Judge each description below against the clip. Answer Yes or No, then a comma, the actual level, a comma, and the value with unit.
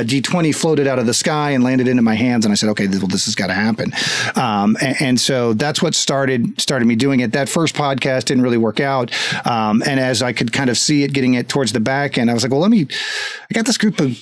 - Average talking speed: No, fast, 275 wpm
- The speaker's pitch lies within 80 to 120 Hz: No, low, 135 Hz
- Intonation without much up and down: No, average, 3.5 semitones